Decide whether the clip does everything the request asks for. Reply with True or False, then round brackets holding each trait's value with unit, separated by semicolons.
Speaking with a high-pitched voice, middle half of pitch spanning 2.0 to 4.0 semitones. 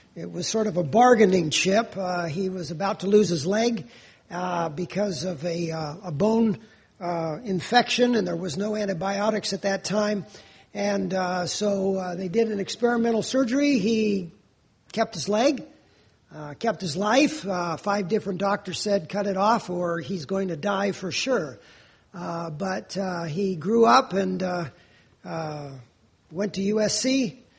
True (195 Hz; 3.2 semitones)